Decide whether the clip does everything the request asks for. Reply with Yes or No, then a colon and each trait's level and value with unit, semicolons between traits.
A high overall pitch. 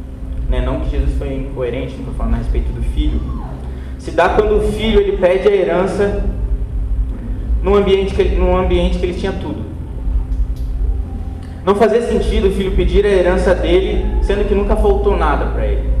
No: medium, 170 Hz